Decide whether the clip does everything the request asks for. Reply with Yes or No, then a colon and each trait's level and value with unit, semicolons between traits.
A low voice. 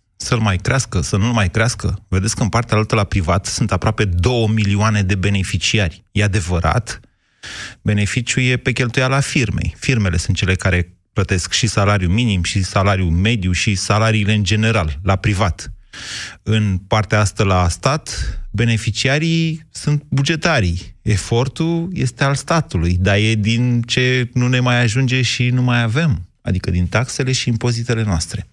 Yes: low, 110 Hz